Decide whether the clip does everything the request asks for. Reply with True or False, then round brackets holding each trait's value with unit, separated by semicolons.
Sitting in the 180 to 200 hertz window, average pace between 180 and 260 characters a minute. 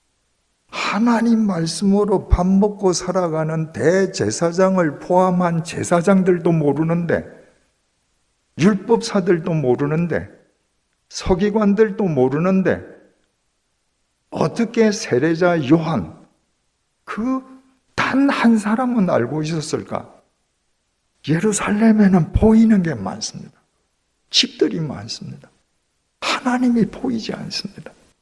True (190 Hz; 215 characters per minute)